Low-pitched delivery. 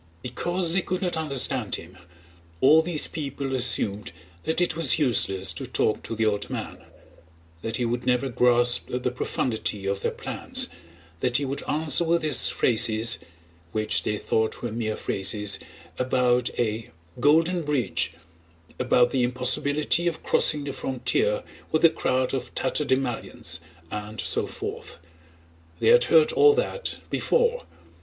Yes: low, 130 Hz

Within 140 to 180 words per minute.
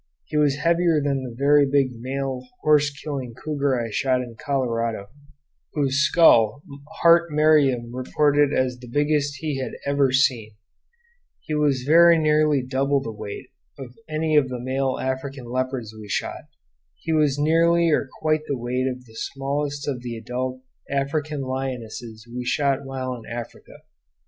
Yes: average, 155 wpm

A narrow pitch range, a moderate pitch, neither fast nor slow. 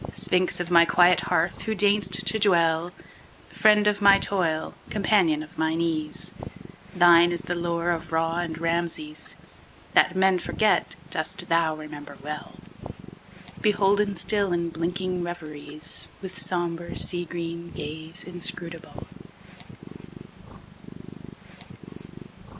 No: narrow, 2.3 semitones; medium, 175 Hz; slow, 100 wpm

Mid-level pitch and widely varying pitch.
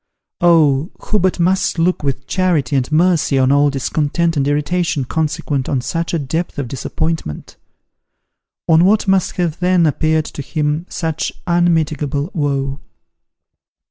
No: medium, 155 Hz; average, 3.5 semitones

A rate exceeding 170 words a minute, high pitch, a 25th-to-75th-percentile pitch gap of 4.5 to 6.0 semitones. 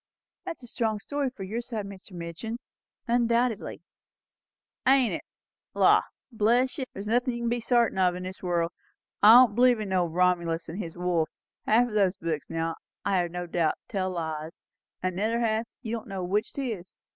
Yes: average, 195 wpm; high, 205 Hz; average, 4.9 semitones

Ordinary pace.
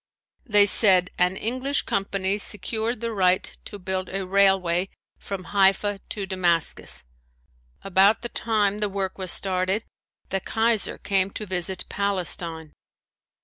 No: slow, 130 wpm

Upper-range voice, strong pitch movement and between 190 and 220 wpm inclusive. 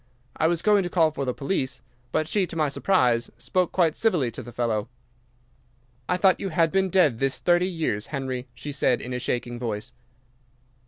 No: medium, 150 Hz; wide, 6.4 semitones; average, 195 wpm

